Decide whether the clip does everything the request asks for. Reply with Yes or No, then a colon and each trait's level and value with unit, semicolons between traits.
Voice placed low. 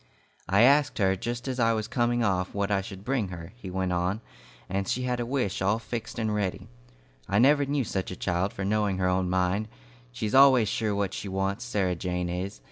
Yes: low, 100 Hz